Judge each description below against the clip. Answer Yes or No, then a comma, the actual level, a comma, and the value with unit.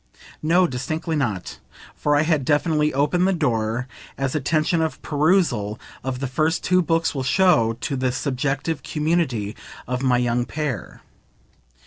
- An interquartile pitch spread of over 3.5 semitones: Yes, average, 4.3 semitones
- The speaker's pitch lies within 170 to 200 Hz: No, medium, 145 Hz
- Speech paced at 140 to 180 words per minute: Yes, average, 145 wpm